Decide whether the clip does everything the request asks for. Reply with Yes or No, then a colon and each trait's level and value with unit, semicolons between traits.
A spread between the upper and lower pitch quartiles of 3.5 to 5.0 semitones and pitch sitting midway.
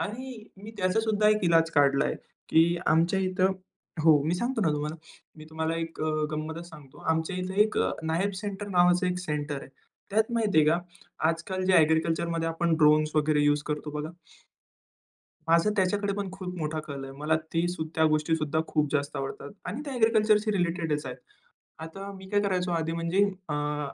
Yes: average, 3.9 semitones; medium, 165 Hz